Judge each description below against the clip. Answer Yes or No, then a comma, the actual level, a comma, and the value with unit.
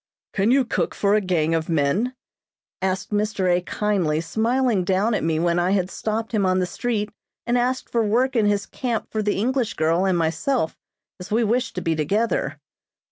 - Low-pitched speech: No, high, 205 Hz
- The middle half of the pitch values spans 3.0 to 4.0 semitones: No, average, 4.5 semitones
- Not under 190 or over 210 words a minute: Yes, average, 195 wpm